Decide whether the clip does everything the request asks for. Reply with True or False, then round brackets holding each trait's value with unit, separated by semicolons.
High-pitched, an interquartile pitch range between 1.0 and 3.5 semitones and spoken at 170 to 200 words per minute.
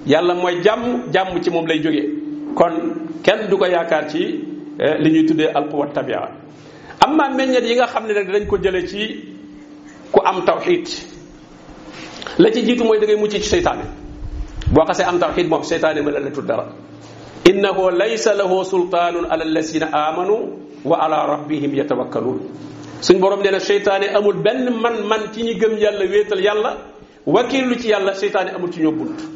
False (200 Hz; 5.6 semitones; 175 wpm)